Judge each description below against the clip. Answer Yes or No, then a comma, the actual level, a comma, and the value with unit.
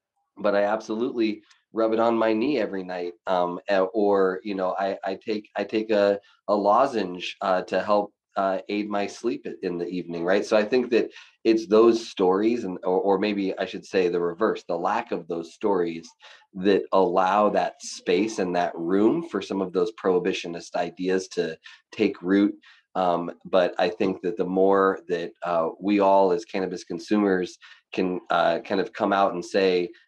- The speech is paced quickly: No, average, 185 wpm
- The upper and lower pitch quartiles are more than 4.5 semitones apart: No, average, 2.8 semitones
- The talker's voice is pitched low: Yes, low, 100 Hz